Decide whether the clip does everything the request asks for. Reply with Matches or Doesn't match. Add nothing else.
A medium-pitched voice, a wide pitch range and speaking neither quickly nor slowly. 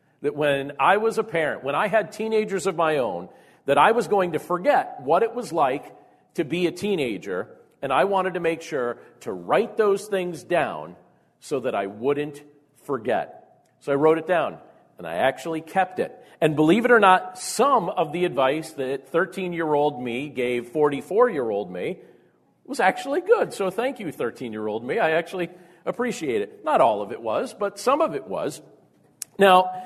Matches